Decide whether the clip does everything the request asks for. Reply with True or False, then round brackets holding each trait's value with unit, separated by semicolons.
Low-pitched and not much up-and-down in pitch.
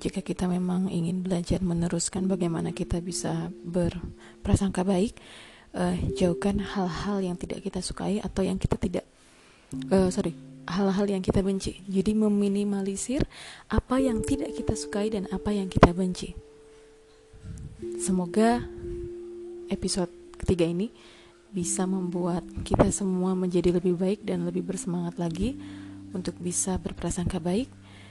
False (180 Hz; 2.3 semitones)